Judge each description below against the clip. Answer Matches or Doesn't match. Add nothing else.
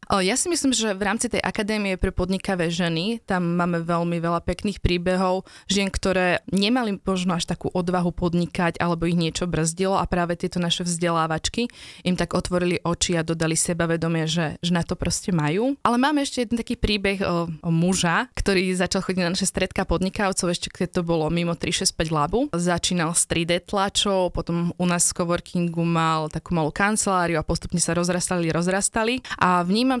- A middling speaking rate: Doesn't match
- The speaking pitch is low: Doesn't match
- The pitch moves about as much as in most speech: Doesn't match